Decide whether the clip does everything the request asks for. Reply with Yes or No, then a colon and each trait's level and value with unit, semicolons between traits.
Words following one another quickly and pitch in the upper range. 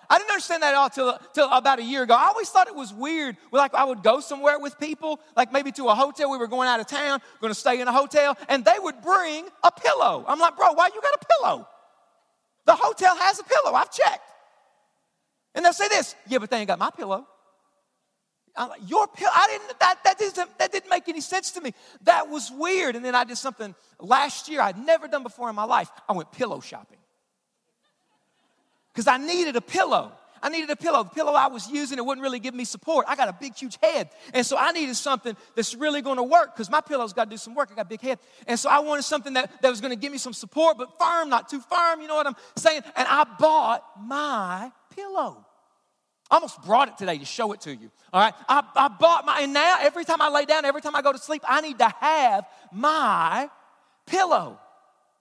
Yes: fast, 240 wpm; very high, 280 Hz